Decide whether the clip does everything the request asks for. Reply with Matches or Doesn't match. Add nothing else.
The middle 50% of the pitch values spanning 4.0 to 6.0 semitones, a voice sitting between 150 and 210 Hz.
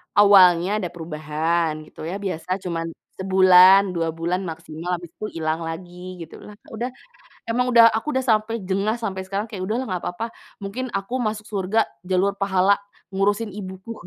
Doesn't match